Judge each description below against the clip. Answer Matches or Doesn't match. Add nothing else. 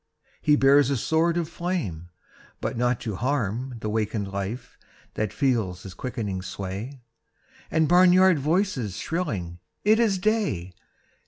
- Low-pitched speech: Matches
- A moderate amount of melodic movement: Doesn't match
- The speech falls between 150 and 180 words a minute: Doesn't match